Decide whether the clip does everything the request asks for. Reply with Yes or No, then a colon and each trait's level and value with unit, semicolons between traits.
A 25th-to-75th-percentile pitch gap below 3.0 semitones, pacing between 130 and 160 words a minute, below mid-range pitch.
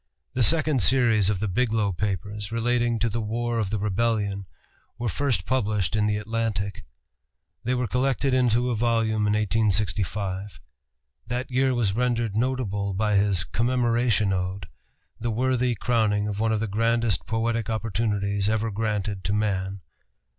Yes: narrow, 2.6 semitones; average, 150 wpm; low, 110 Hz